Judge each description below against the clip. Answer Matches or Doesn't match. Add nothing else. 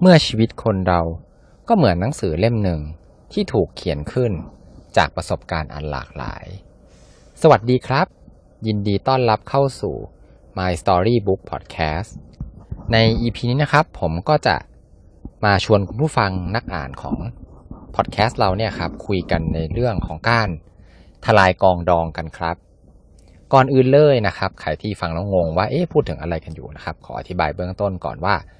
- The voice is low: Matches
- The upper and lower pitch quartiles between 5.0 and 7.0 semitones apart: Matches